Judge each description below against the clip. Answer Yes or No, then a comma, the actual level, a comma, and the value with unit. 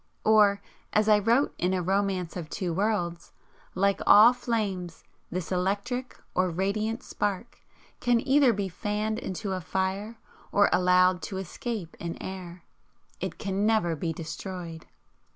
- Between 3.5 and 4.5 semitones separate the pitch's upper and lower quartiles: No, average, 3.0 semitones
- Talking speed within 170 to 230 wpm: No, average, 145 wpm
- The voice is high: Yes, high, 195 Hz